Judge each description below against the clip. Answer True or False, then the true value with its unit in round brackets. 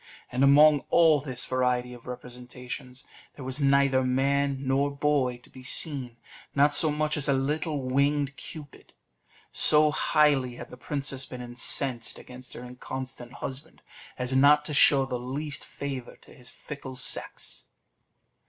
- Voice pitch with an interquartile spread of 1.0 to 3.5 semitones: True (2.4 semitones)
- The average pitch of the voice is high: False (135 Hz)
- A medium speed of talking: True (150 wpm)